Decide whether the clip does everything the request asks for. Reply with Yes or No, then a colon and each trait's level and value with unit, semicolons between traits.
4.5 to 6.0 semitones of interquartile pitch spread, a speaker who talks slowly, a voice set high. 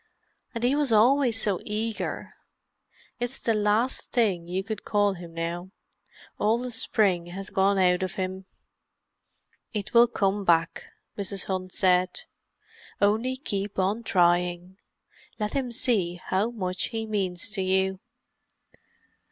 No: average, 3.4 semitones; slow, 130 wpm; high, 200 Hz